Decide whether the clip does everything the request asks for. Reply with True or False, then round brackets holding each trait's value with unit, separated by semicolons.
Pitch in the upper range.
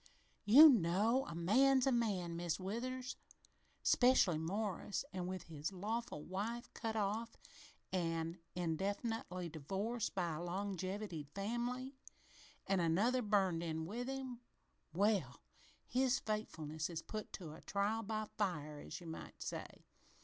True (200 Hz)